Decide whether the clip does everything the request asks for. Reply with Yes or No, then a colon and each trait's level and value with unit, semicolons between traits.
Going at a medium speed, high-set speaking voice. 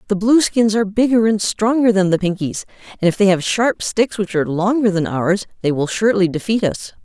No: fast, 215 wpm; high, 205 Hz